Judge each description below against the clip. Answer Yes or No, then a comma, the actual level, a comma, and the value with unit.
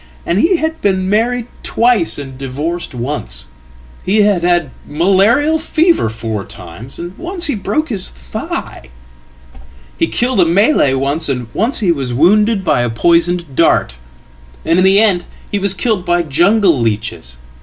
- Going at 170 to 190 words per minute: No, average, 145 wpm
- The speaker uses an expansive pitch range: Yes, wide, 7.8 semitones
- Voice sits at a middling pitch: Yes, medium, 175 Hz